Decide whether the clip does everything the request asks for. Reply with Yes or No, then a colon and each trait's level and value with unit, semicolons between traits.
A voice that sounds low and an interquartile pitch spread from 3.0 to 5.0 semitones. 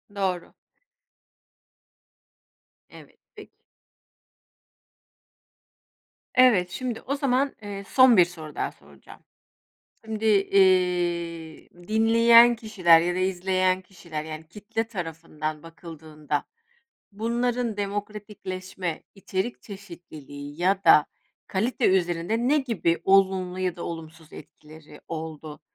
No: medium, 185 Hz; average, 4.6 semitones